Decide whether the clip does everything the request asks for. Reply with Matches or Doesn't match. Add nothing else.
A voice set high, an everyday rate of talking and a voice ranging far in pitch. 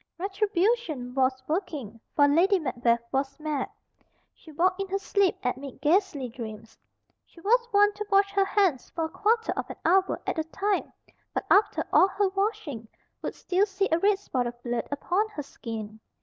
Matches